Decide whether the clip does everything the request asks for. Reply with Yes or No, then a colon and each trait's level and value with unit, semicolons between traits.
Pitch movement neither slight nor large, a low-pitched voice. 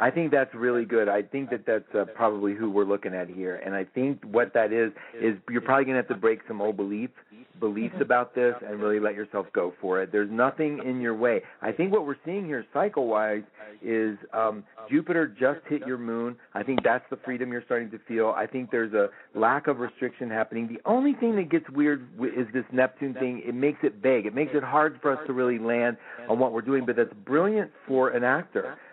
Yes: average, 3.8 semitones; low, 125 Hz